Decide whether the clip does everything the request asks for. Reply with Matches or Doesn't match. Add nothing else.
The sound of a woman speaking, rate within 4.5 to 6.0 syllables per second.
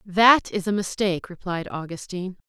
Matches